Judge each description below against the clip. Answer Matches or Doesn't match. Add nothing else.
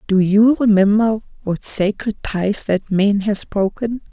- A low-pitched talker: Doesn't match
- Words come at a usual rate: Matches